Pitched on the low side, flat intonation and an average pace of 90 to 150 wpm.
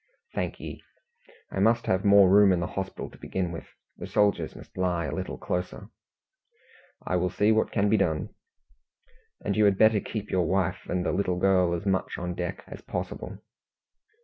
No: very low, 95 Hz; narrow, 2.3 semitones; average, 185 wpm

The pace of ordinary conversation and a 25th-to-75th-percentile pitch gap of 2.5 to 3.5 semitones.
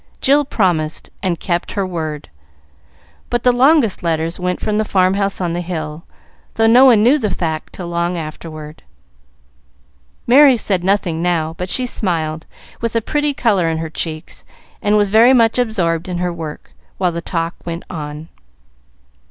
No: average, 170 wpm; average, 5.2 semitones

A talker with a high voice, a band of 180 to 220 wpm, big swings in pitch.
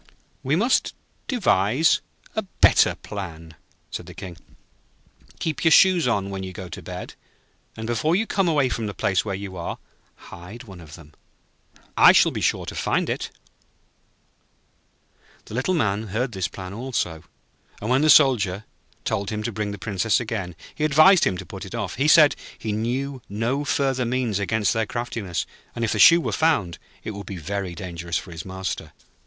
No: low, 110 Hz; average, 185 wpm; wide, 6.1 semitones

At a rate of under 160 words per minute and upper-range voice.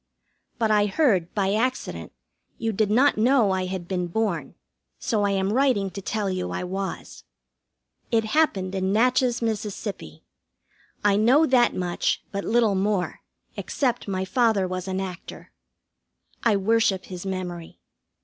Yes: average, 145 wpm; high, 205 Hz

